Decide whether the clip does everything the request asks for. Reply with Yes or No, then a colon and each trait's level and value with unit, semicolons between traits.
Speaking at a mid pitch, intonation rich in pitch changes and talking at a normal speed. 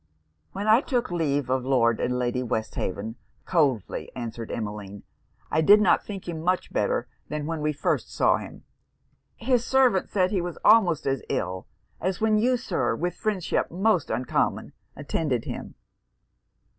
Yes: medium, 160 Hz; wide, 8.7 semitones; average, 155 wpm